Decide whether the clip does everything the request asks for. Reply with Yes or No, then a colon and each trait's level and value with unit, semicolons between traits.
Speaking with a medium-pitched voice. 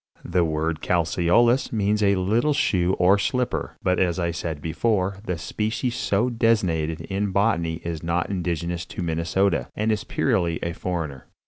No: very low, 90 Hz